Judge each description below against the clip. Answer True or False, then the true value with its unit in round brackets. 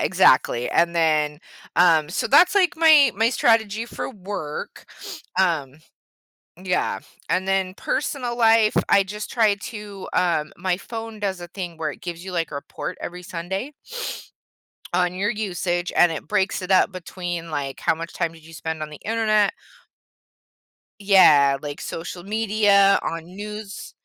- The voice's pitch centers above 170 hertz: True (185 Hz)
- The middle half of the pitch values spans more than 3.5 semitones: True (4.1 semitones)